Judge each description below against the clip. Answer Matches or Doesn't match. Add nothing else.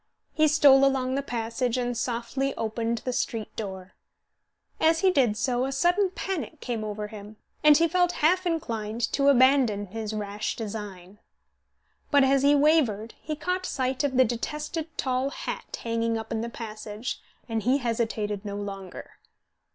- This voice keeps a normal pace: Matches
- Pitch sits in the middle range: Doesn't match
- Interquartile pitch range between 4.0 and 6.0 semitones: Matches